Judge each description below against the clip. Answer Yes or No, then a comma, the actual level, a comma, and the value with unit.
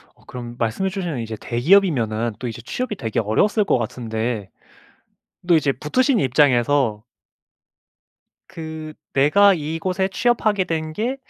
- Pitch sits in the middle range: Yes, medium, 150 Hz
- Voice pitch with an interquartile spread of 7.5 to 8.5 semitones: Yes, wide, 8.2 semitones